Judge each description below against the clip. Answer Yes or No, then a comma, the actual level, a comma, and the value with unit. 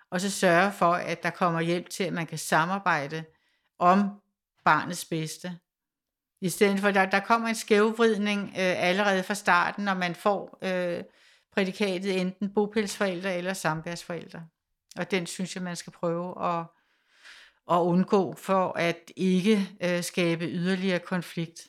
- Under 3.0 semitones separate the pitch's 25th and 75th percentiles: Yes, narrow, 2.5 semitones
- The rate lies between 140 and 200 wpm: Yes, average, 150 wpm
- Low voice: No, medium, 180 Hz